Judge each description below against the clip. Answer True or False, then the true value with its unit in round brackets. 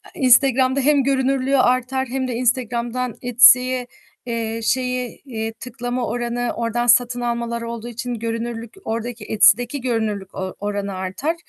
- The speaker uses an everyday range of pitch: False (1.8 semitones)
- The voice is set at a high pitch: True (240 Hz)